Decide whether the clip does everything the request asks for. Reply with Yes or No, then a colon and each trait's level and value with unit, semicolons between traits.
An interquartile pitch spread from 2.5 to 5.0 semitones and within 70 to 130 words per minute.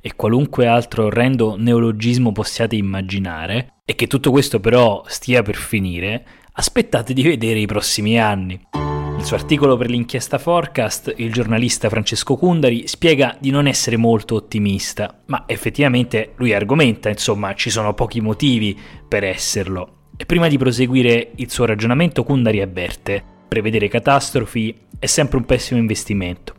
No: average, 3.5 semitones; average, 145 wpm